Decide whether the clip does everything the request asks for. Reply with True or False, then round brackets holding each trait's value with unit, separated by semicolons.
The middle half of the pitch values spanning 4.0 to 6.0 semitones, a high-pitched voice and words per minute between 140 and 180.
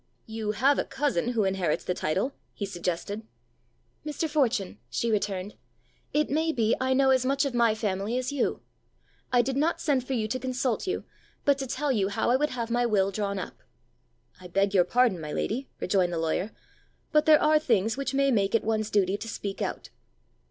False (5.2 semitones; 230 Hz; 200 wpm)